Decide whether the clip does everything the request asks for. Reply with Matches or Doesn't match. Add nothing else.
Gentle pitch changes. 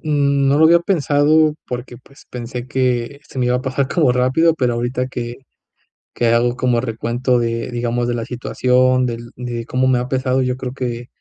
Matches